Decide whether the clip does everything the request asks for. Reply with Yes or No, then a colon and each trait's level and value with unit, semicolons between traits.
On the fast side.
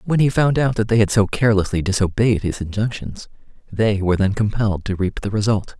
Yes: fast, 215 wpm